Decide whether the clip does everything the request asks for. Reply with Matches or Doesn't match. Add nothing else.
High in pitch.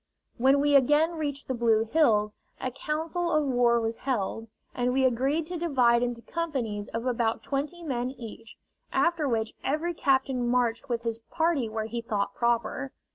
Matches